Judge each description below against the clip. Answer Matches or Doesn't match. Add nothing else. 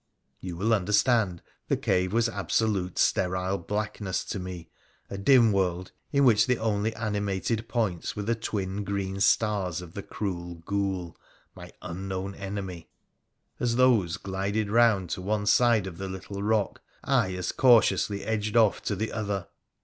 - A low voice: Matches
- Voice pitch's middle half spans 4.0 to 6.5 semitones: Doesn't match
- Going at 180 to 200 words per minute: Doesn't match